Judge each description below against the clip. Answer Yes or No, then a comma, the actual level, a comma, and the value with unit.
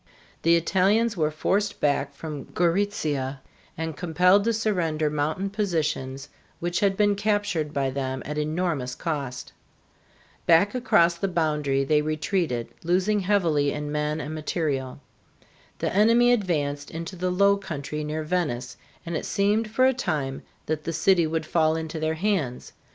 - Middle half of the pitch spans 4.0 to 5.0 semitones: Yes, average, 4.6 semitones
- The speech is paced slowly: No, average, 150 wpm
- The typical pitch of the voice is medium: Yes, medium, 160 Hz